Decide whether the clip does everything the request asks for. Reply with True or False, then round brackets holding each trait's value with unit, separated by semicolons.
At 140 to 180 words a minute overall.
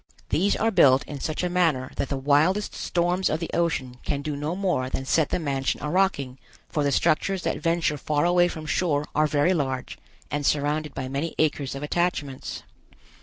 False (195 wpm)